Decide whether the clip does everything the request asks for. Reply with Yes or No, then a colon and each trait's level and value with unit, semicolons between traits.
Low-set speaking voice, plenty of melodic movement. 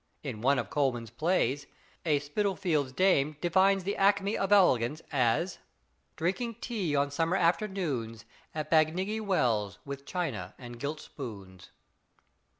No: medium, 155 Hz; wide, 6.8 semitones